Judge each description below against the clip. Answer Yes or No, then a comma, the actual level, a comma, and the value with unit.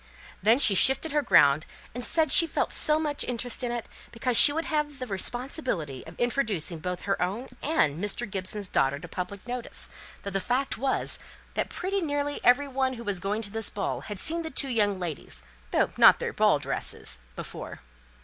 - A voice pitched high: Yes, high, 235 Hz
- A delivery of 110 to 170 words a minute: No, average, 195 wpm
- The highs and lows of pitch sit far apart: Yes, wide, 6.2 semitones